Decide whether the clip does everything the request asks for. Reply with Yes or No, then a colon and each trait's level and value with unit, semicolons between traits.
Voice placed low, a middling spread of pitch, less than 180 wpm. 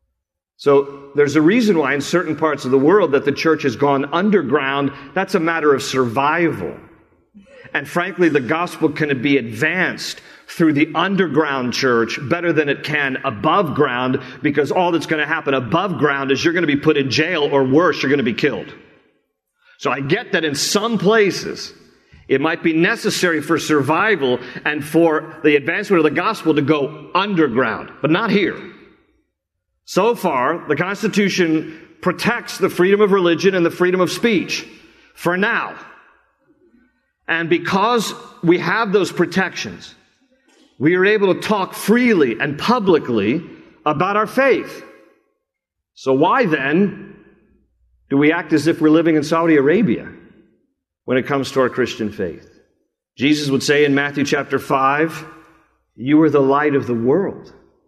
No: medium, 155 Hz; average, 4.5 semitones; average, 160 wpm